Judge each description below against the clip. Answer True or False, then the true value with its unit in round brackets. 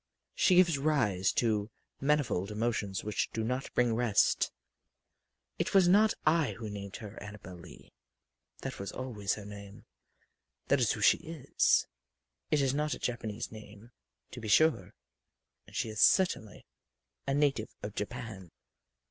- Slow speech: False (150 wpm)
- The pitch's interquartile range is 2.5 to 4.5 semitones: False (5.4 semitones)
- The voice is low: True (115 Hz)